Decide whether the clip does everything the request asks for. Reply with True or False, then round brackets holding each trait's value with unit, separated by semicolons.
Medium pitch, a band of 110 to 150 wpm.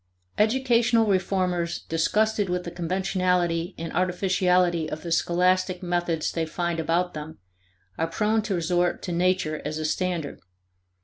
True (180 Hz; 140 wpm)